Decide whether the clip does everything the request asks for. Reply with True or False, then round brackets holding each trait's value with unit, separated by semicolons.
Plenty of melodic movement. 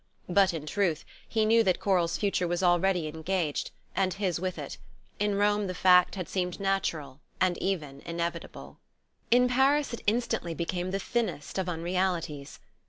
False (2.9 semitones)